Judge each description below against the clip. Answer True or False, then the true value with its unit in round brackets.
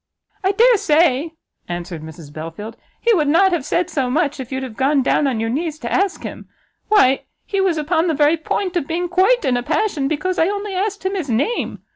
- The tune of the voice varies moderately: False (6.2 semitones)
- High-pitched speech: True (310 Hz)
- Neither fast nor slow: False (220 wpm)